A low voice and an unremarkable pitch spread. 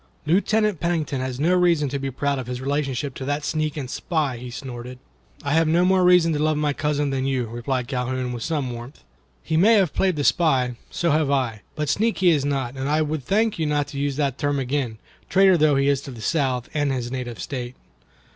No: medium, 145 Hz; average, 3.4 semitones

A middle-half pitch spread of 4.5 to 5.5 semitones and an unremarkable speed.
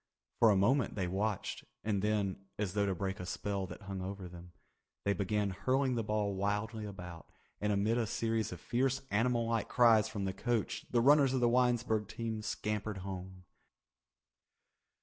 No: average, 2.9 semitones; average, 175 wpm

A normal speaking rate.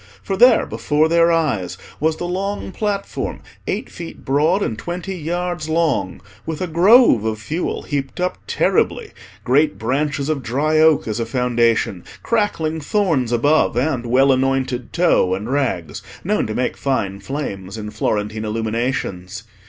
Yes: average, 150 wpm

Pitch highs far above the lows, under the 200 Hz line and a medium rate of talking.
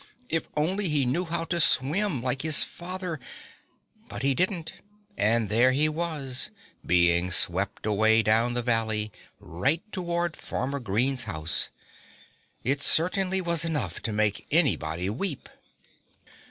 No: wide, 7.3 semitones; low, 135 Hz; slow, 130 wpm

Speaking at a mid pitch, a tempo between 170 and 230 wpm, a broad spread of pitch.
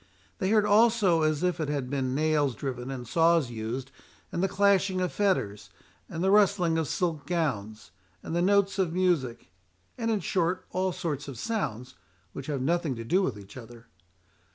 Yes: medium, 160 Hz; average, 180 wpm; wide, 6.3 semitones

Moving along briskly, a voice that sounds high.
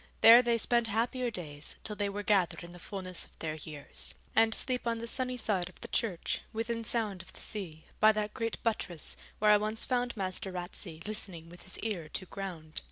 Yes: fast, 210 wpm; high, 205 Hz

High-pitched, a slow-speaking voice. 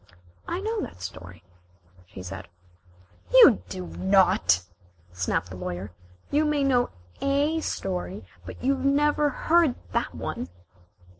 Yes: high, 245 Hz; slow, 125 wpm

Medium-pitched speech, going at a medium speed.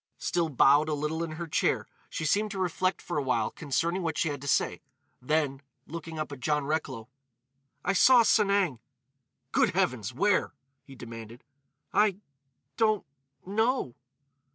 Yes: medium, 155 Hz; average, 145 wpm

